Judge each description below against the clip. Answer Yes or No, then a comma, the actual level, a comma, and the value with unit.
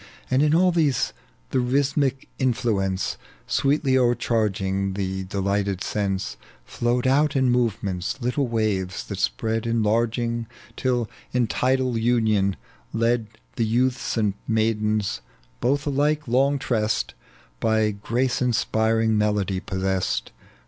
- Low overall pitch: Yes, low, 115 Hz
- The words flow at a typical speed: No, slow, 115 wpm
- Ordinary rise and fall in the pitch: Yes, average, 3.9 semitones